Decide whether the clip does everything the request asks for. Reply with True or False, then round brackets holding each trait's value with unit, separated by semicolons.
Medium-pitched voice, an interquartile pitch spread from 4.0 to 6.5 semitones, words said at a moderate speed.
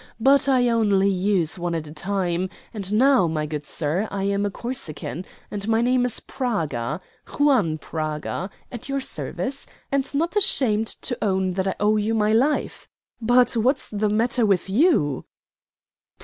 False (210 Hz; 5.5 semitones; 165 wpm)